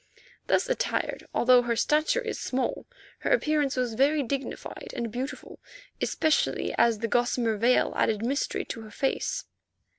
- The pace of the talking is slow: No, average, 145 wpm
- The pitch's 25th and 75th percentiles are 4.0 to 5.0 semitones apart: Yes, average, 4.4 semitones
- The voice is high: Yes, very high, 255 Hz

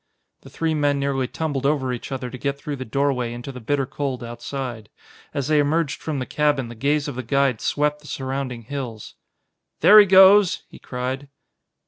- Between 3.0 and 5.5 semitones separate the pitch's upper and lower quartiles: No, narrow, 2.6 semitones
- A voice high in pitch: No, medium, 140 Hz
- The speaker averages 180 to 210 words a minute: Yes, average, 190 wpm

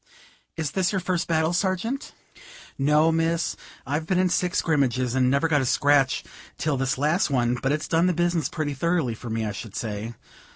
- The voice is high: No, medium, 150 Hz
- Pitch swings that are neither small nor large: Yes, average, 4.6 semitones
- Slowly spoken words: No, average, 195 wpm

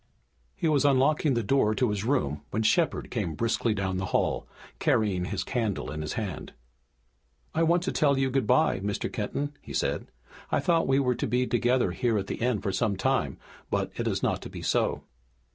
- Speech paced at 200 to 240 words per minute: Yes, fast, 205 wpm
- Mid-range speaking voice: No, low, 120 Hz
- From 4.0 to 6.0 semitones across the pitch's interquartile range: Yes, average, 5.3 semitones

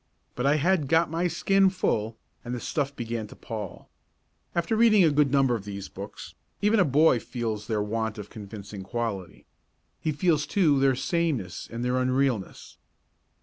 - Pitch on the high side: No, low, 130 Hz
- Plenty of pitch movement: Yes, wide, 6.4 semitones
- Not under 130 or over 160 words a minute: No, average, 175 wpm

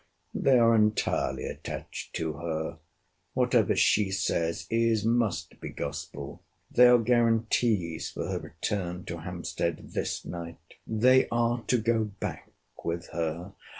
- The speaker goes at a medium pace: No, slow, 130 wpm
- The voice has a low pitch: Yes, low, 105 Hz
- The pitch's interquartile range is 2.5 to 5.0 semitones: No, wide, 5.6 semitones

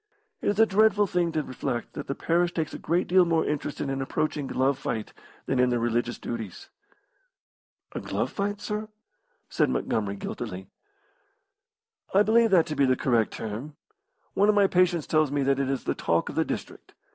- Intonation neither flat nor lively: No, wide, 6.4 semitones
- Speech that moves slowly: No, average, 190 wpm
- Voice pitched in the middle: Yes, medium, 150 Hz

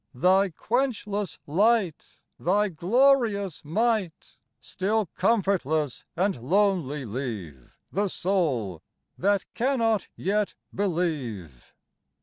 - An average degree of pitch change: No, wide, 5.9 semitones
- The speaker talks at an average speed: No, slow, 85 wpm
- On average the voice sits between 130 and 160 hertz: No, high, 190 Hz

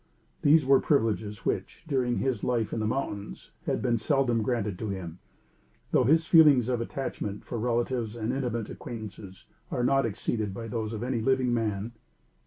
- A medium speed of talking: Yes, average, 170 wpm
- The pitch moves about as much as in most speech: Yes, average, 3.3 semitones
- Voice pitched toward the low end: Yes, low, 120 Hz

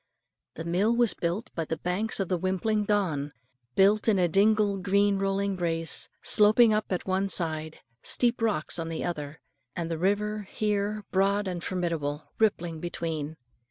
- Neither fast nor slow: Yes, average, 160 wpm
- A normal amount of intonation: Yes, average, 3.9 semitones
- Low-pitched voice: No, high, 190 Hz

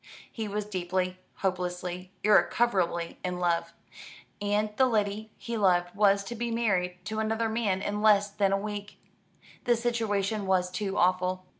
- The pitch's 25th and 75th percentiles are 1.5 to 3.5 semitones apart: Yes, average, 2.9 semitones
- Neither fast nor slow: Yes, average, 150 wpm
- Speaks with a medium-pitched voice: No, high, 200 Hz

